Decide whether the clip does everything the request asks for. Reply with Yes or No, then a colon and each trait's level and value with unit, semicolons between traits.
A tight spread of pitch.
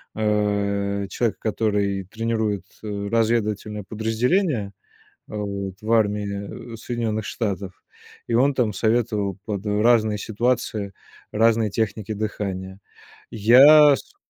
Yes: narrow, 2.2 semitones